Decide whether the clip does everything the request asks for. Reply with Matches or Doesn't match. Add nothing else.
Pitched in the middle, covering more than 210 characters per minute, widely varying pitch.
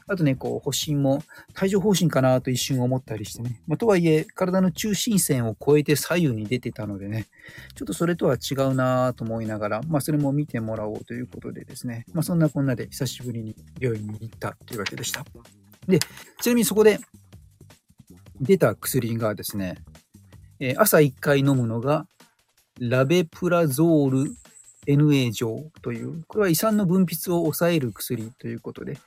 Doesn't match